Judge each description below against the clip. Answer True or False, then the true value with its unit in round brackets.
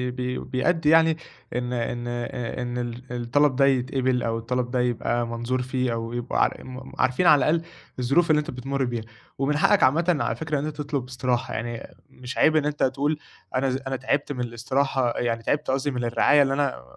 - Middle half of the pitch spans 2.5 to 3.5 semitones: True (2.9 semitones)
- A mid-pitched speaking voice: False (130 Hz)